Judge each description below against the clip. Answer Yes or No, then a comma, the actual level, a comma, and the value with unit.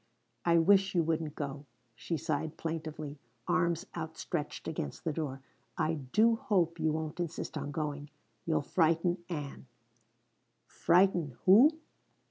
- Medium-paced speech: No, slow, 125 wpm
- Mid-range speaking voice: Yes, medium, 160 Hz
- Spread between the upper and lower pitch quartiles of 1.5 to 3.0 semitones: Yes, narrow, 2.5 semitones